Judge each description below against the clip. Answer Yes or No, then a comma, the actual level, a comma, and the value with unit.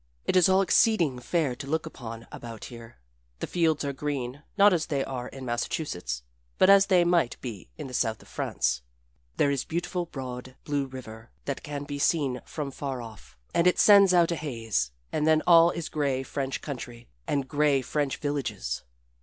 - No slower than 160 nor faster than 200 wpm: Yes, average, 190 wpm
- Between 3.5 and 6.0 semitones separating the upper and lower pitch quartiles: Yes, average, 4.9 semitones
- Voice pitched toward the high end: No, medium, 140 Hz